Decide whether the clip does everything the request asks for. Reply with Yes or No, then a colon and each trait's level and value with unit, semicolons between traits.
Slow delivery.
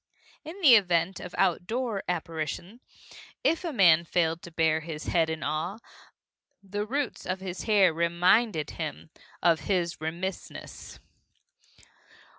Yes: slow, 125 wpm